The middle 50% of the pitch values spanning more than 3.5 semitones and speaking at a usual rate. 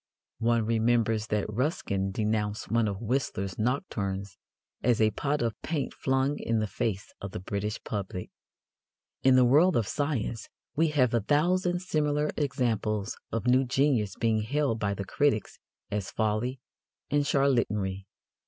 Yes: average, 4.8 semitones; average, 145 wpm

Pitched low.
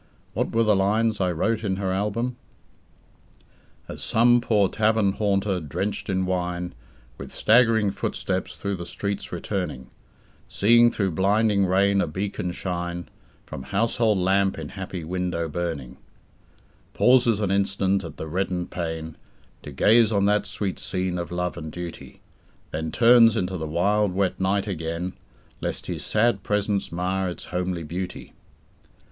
Yes: very low, 95 Hz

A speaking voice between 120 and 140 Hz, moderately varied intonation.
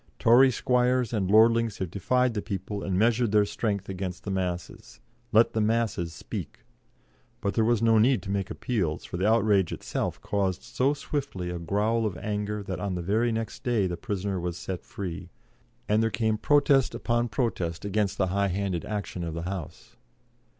No: low, 105 Hz; average, 3.6 semitones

